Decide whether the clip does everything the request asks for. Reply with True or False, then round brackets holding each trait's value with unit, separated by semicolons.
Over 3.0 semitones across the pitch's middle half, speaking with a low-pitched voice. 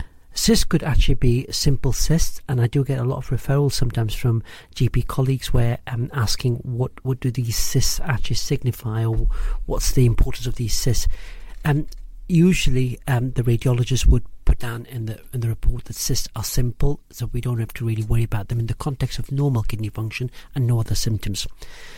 False (2.6 semitones; 125 Hz)